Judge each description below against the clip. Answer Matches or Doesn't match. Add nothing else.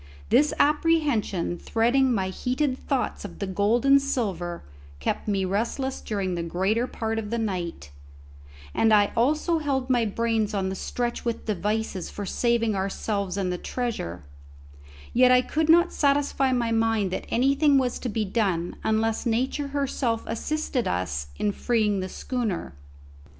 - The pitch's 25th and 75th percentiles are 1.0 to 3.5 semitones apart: Doesn't match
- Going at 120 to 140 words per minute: Doesn't match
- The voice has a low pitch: Doesn't match